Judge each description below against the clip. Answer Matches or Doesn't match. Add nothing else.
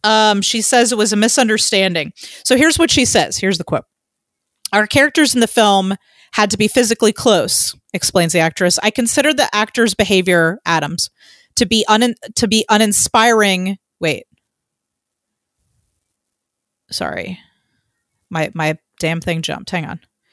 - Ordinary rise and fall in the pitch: Matches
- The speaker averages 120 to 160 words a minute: Matches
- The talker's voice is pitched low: Doesn't match